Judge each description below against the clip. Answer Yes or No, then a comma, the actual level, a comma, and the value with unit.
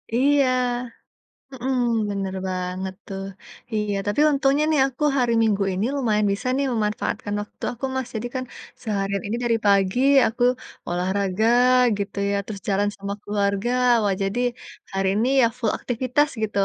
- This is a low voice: No, high, 210 Hz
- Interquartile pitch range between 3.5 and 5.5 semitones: Yes, average, 3.8 semitones